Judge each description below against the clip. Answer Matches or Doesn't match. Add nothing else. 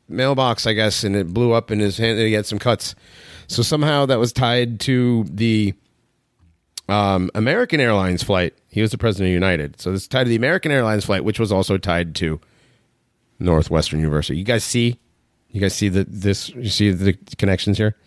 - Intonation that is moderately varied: Matches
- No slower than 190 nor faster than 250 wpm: Matches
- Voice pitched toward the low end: Matches